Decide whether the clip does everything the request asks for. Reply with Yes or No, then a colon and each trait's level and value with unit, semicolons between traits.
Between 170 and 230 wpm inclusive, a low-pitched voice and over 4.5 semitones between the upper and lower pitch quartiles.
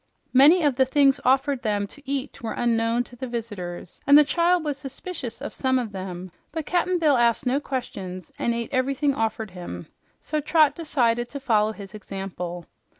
No: average, 185 wpm; very high, 250 Hz; average, 4.9 semitones